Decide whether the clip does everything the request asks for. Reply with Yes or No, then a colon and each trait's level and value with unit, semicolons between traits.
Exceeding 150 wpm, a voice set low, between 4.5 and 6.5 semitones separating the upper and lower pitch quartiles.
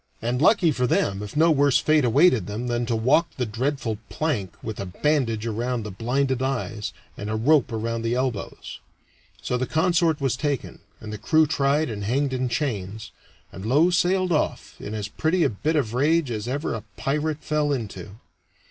Yes: average, 190 wpm; low, 125 Hz; average, 5.3 semitones